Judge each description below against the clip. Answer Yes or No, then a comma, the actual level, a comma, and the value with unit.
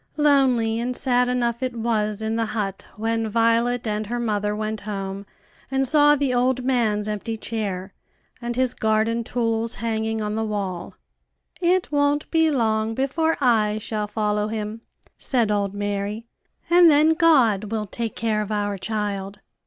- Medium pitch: No, high, 225 Hz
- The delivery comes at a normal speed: Yes, average, 160 wpm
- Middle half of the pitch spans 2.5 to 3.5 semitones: Yes, average, 2.9 semitones